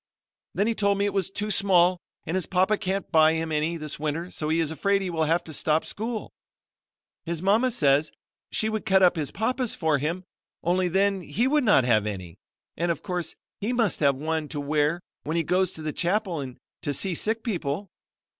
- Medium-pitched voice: Yes, medium, 175 Hz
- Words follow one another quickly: Yes, fast, 210 wpm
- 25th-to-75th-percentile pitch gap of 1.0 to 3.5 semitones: No, average, 4.4 semitones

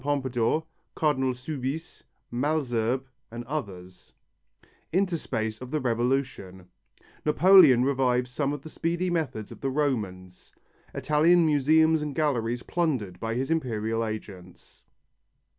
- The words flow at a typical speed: No, slow, 110 wpm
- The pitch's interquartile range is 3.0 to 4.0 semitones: No, average, 5.1 semitones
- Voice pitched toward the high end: No, low, 130 Hz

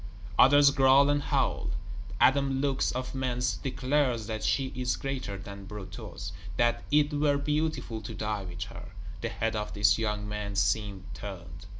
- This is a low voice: Yes, low, 120 Hz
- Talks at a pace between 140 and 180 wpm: Yes, average, 160 wpm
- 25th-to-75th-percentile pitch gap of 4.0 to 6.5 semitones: Yes, average, 5.0 semitones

